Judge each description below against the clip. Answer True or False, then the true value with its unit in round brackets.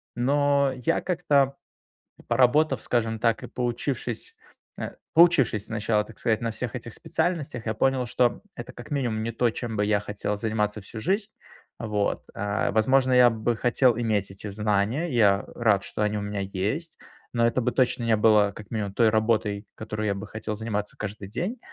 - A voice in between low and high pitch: False (115 Hz)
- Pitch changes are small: False (3.2 semitones)